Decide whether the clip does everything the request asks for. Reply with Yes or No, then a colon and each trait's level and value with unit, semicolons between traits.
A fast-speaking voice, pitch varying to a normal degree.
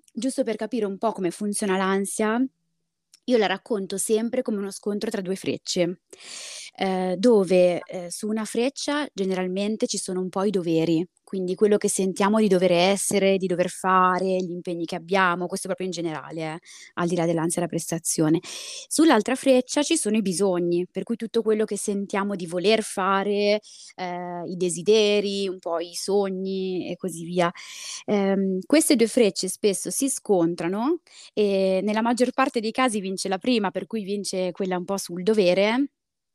Yes: fast, 175 wpm; average, 3.2 semitones